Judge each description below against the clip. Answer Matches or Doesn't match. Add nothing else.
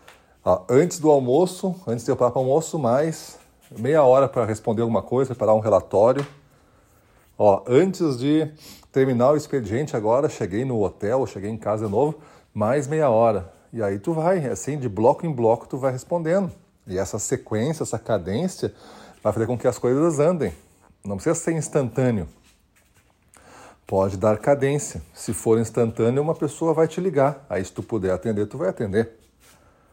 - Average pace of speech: Matches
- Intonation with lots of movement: Matches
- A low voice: Matches